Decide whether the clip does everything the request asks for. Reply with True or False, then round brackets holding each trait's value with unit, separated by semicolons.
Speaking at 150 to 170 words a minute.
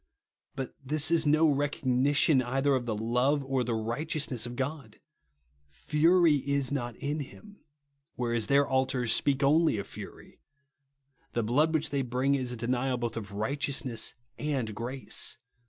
True (155 wpm)